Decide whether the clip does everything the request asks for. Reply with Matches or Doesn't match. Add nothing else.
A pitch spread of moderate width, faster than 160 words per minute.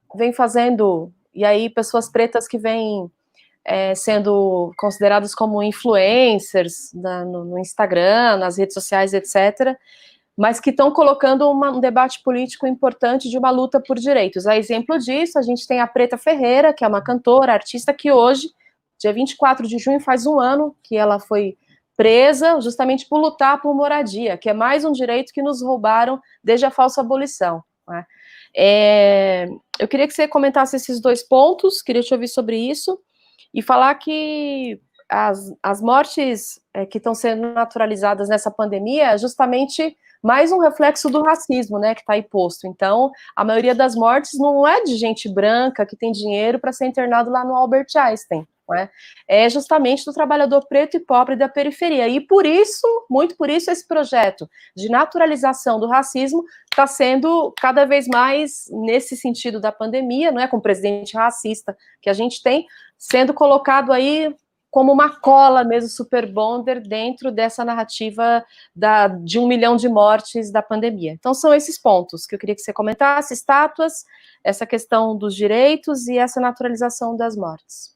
Matches